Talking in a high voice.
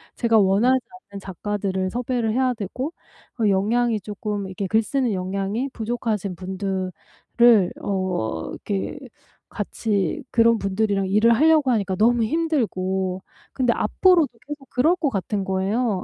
Yes: high, 210 Hz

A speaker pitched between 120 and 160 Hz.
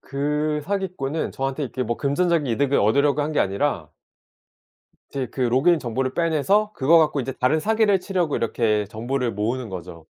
Yes: medium, 140 Hz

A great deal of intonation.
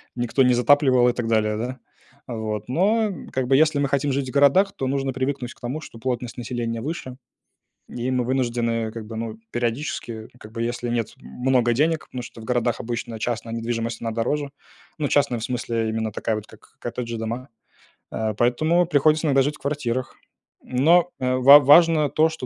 No: average, 3.4 semitones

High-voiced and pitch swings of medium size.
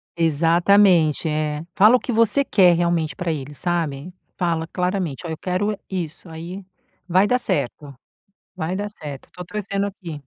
No: medium, 175 Hz; average, 3.7 semitones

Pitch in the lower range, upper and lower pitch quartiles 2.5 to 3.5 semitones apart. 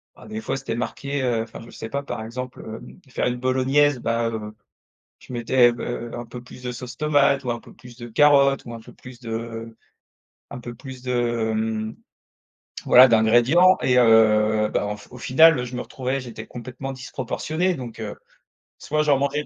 Yes: low, 125 Hz; average, 2.8 semitones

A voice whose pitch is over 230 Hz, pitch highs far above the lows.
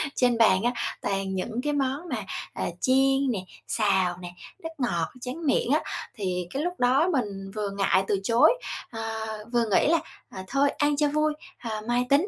Yes: high, 240 Hz; wide, 6.1 semitones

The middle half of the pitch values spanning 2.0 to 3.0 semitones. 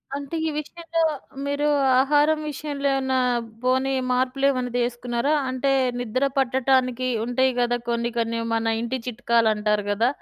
Yes: average, 2.7 semitones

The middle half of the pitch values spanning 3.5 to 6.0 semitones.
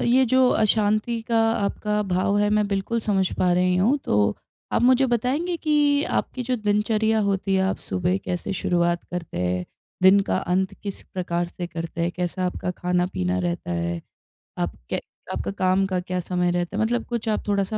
Yes: average, 3.8 semitones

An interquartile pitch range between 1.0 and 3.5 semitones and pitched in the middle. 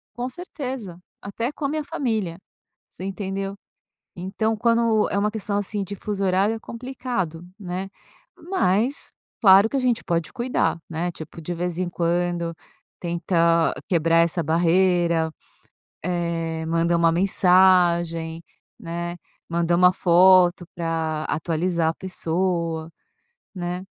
Yes: average, 3.2 semitones; medium, 180 Hz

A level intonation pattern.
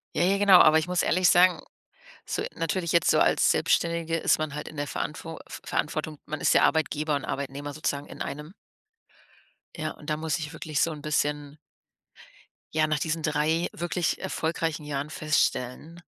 Yes: narrow, 1.9 semitones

